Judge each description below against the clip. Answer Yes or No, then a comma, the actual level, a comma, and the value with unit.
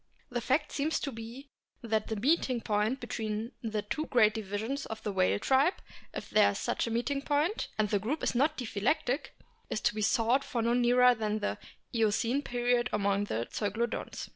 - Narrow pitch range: No, average, 3.6 semitones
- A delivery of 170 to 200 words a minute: Yes, average, 190 wpm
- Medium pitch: No, high, 235 Hz